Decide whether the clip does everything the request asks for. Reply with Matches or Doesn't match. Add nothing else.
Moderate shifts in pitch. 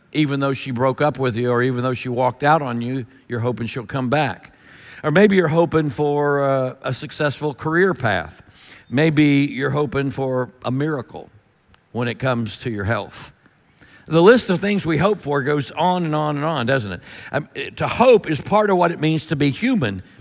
Matches